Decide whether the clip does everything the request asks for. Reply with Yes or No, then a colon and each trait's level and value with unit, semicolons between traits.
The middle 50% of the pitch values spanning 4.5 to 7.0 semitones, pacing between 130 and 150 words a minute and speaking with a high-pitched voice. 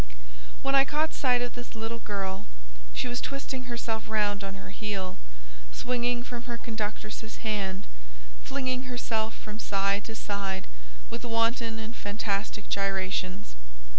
No: average, 3.4 semitones; slow, 135 wpm; high, 220 Hz